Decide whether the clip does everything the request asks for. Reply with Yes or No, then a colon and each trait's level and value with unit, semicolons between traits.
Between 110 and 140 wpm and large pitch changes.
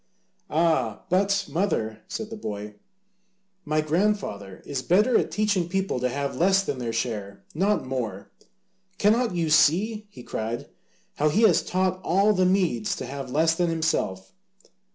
No: average, 155 wpm; wide, 7.6 semitones